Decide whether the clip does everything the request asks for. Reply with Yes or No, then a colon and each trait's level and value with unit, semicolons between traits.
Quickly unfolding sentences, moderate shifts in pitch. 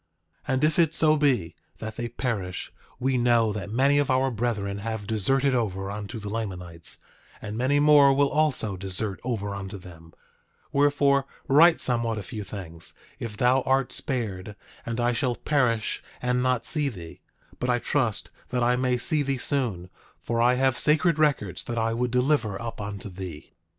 No: average, 175 wpm; average, 4.7 semitones